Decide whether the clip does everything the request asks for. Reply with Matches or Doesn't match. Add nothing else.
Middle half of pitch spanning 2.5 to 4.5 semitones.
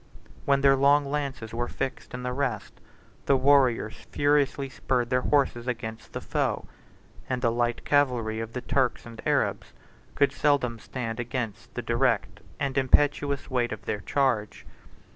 Matches